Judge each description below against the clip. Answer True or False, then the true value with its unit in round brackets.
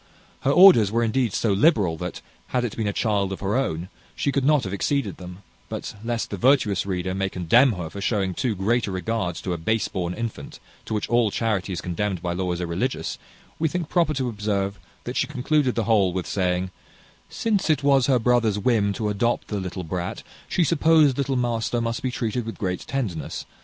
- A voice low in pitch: True (110 Hz)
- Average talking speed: False (210 wpm)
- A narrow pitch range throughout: False (5.0 semitones)